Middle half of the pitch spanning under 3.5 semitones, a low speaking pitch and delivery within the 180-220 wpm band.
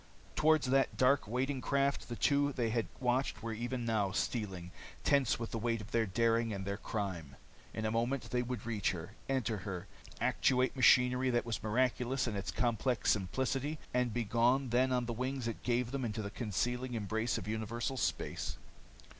Yes: average, 2.8 semitones; low, 120 Hz; average, 185 wpm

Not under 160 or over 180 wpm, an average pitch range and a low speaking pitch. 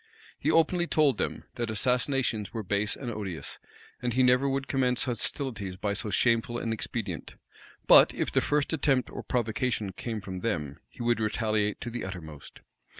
Yes: average, 170 wpm; average, 3.7 semitones; low, 115 Hz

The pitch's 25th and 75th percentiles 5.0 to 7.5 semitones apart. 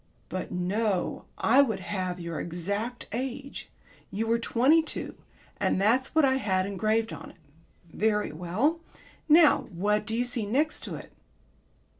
Yes: wide, 5.5 semitones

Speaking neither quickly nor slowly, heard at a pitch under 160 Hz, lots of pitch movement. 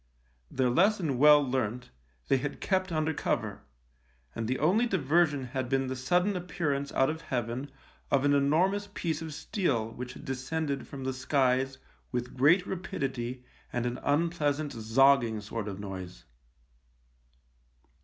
No: average, 145 wpm; low, 135 Hz; average, 4.1 semitones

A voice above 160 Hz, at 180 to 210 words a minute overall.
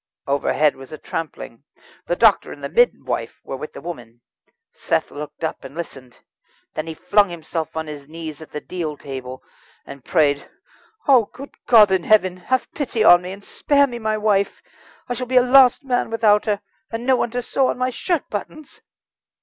Yes: high, 190 Hz; average, 190 wpm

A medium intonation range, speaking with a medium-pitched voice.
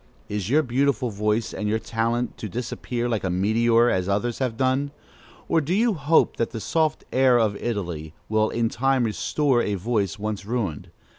No: average, 3.8 semitones; low, 115 Hz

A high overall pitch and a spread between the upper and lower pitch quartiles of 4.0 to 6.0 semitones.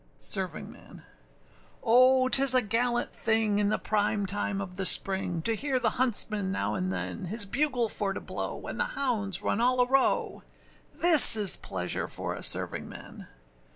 Yes: high, 220 Hz; average, 4.3 semitones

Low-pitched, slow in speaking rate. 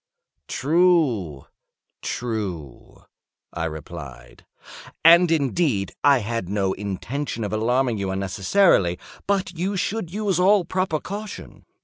Yes: low, 125 Hz; slow, 95 wpm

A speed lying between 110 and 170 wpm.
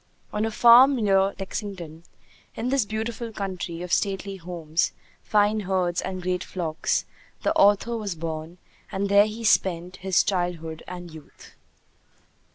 Yes: average, 140 wpm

